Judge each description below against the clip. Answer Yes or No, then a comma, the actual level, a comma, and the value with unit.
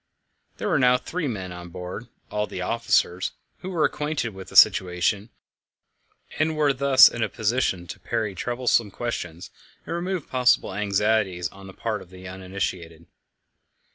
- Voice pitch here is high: No, low, 105 Hz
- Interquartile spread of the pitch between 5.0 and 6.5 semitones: Yes, average, 5.3 semitones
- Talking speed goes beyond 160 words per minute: No, average, 155 wpm